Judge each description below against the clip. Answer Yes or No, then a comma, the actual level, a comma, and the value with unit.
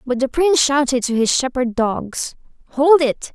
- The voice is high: Yes, very high, 265 Hz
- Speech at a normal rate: Yes, average, 180 wpm